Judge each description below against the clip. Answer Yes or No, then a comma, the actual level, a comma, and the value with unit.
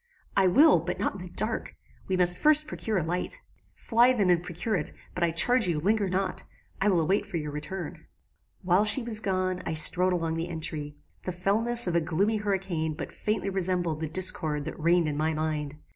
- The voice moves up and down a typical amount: Yes, average, 3.8 semitones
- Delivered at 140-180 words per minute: No, fast, 205 wpm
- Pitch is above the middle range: No, medium, 180 Hz